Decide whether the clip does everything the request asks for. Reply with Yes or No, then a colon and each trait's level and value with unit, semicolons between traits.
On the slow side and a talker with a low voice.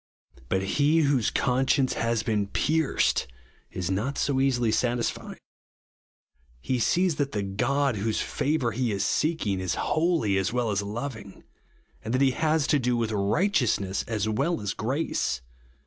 No: average, 150 wpm; low, 120 Hz